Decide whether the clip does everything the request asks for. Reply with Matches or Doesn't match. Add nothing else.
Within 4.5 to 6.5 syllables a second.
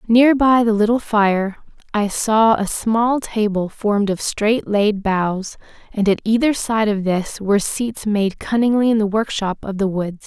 Doesn't match